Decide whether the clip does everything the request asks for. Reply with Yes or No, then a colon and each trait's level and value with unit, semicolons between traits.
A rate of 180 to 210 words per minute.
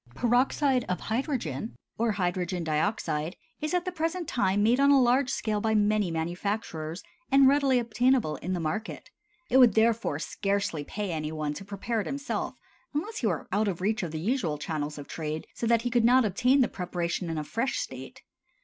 Yes: average, 195 wpm